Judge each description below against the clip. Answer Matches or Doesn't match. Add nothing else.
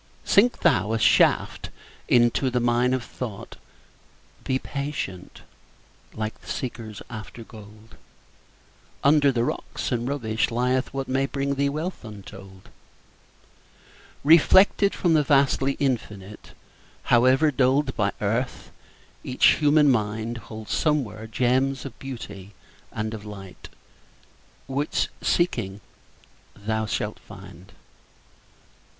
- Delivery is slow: Matches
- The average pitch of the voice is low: Matches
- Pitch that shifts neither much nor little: Matches